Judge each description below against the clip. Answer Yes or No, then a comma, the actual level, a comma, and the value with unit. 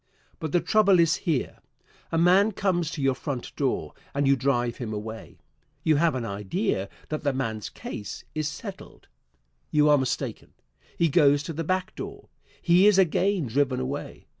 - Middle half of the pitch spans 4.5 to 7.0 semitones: Yes, average, 5.2 semitones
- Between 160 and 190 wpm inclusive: Yes, average, 170 wpm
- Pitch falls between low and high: Yes, medium, 150 Hz